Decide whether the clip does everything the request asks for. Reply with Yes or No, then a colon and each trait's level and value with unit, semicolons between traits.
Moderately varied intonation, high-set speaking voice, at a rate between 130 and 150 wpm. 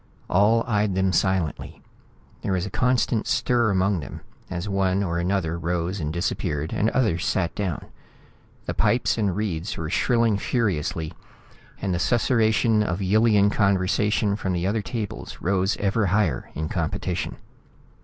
No: average, 3.4 semitones; very low, 95 Hz; average, 145 wpm